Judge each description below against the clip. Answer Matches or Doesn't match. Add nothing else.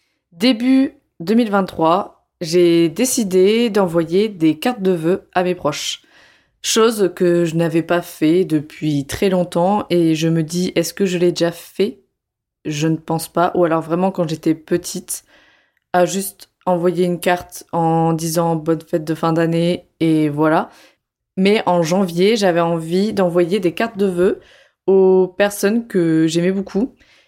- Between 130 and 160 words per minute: Matches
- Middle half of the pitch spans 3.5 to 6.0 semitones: Doesn't match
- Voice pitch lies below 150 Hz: Doesn't match